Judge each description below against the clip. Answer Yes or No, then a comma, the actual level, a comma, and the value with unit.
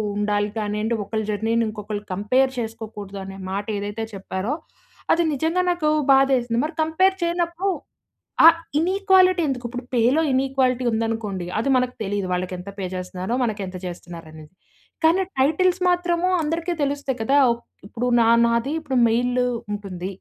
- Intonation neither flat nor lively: No, wide, 6.8 semitones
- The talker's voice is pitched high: Yes, high, 235 Hz